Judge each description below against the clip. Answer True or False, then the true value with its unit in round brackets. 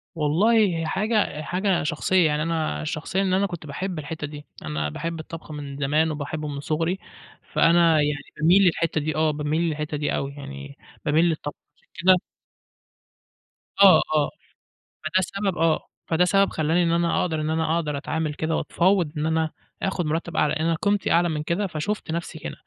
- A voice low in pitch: False (160 Hz)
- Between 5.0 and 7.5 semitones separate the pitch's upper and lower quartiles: False (2.6 semitones)